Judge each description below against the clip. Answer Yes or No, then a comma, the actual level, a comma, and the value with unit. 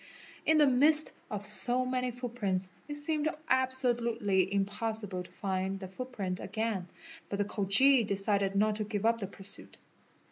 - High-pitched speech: Yes, high, 215 Hz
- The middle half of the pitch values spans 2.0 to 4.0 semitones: No, average, 4.4 semitones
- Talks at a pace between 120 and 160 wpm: Yes, average, 155 wpm